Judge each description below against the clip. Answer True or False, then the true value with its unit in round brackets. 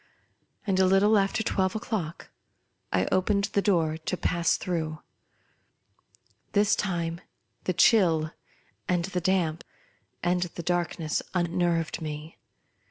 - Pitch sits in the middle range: True (175 Hz)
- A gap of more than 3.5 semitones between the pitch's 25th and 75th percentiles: False (2.8 semitones)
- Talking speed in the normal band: False (115 wpm)